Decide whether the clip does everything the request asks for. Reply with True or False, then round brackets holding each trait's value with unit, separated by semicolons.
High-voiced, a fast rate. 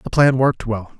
False (120 Hz; 240 wpm)